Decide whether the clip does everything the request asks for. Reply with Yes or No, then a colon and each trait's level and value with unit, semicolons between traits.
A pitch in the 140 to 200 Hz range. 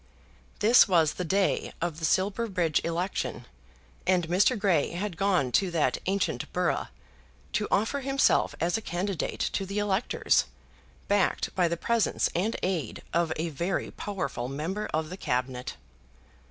Yes: medium, 185 Hz